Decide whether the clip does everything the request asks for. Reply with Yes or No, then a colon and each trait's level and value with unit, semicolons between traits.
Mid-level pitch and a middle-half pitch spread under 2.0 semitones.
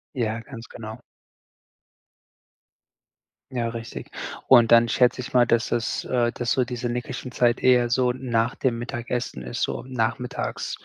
No: low, 120 Hz; narrow, 1.2 semitones